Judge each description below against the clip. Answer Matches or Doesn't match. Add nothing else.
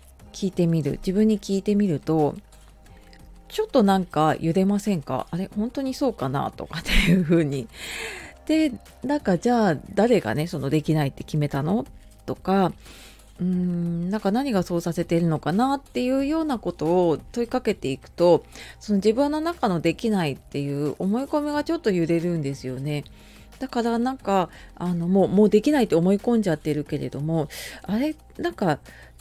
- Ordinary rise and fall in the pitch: Doesn't match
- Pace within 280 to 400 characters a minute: Matches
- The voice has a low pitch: Doesn't match